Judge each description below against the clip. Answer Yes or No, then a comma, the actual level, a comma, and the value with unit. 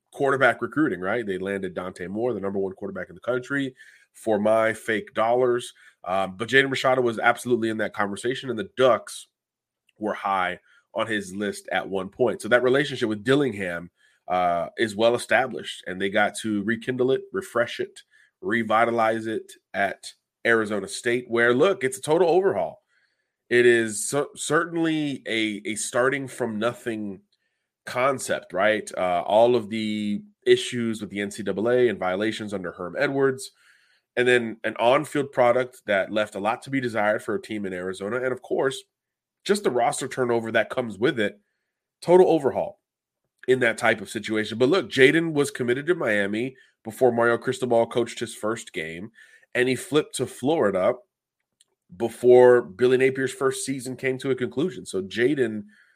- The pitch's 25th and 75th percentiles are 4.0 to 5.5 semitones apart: No, average, 3.6 semitones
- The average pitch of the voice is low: Yes, low, 120 Hz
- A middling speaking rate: Yes, average, 165 wpm